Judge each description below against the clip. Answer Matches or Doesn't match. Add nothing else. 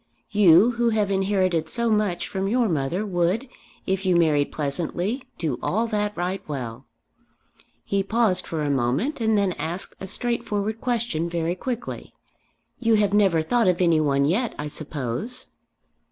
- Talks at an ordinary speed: Matches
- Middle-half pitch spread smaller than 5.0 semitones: Doesn't match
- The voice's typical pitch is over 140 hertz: Matches